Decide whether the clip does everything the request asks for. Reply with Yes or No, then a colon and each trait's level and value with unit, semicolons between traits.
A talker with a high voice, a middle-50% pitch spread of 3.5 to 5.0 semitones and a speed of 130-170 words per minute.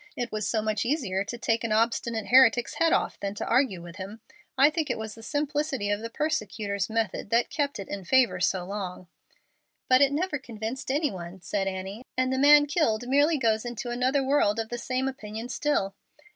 No: high, 230 Hz; average, 4.7 semitones; fast, 205 wpm